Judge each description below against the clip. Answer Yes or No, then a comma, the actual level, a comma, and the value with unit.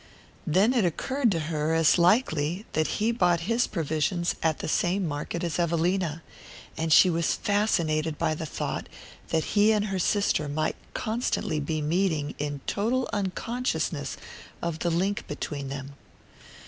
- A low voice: No, medium, 170 Hz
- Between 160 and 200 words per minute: No, average, 150 wpm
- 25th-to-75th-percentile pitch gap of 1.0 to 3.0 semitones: No, average, 4.6 semitones